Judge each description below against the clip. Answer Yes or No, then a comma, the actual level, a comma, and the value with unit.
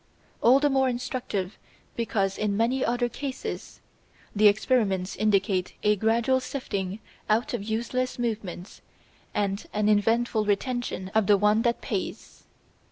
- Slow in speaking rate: Yes, slow, 130 wpm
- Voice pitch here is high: Yes, high, 220 Hz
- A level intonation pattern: No, average, 3.2 semitones